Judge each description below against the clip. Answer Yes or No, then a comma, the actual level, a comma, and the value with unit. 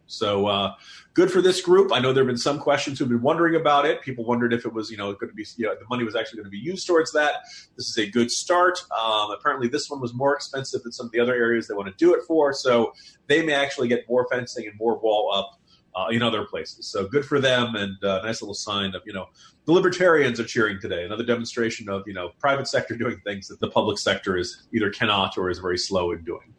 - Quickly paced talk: Yes, fast, 270 wpm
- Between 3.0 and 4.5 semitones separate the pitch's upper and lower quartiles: No, average, 5.2 semitones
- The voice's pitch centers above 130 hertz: No, low, 120 Hz